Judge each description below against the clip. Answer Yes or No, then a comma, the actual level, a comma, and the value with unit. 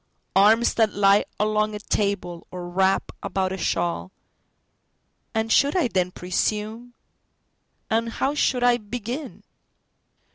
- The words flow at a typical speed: No, slow, 110 wpm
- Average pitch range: Yes, average, 3.8 semitones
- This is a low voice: No, high, 210 Hz